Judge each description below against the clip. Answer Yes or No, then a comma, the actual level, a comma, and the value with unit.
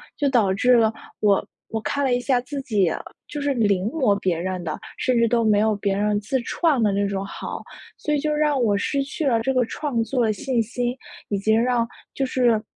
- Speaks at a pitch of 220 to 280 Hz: Yes, high, 230 Hz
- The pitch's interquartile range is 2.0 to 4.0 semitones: No, average, 4.4 semitones